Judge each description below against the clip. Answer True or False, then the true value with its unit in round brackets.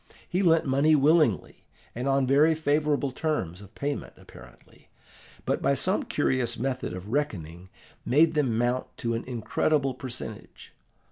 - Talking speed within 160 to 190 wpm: False (140 wpm)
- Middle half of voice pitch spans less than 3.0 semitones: False (4.4 semitones)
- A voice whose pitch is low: True (130 Hz)